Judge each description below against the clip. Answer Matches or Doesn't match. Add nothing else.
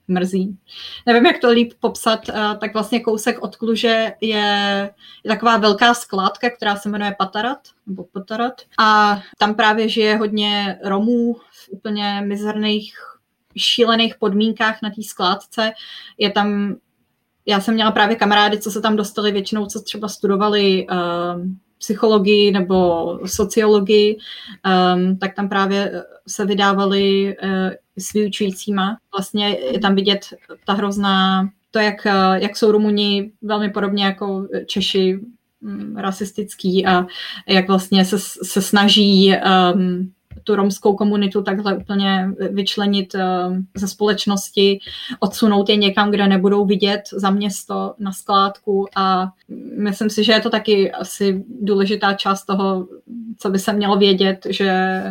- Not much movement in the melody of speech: Matches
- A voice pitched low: Doesn't match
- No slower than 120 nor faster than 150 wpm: Matches